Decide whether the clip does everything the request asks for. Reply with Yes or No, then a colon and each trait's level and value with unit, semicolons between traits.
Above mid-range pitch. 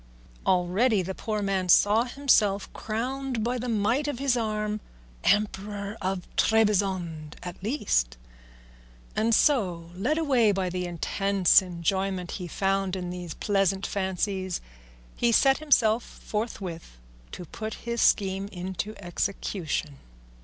Yes: high, 200 Hz